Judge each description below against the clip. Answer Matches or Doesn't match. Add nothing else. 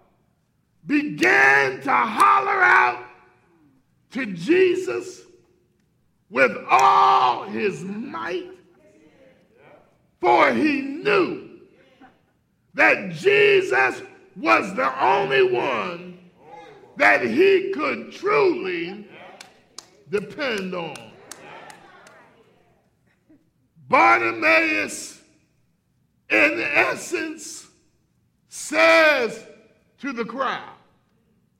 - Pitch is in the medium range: Doesn't match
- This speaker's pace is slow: Matches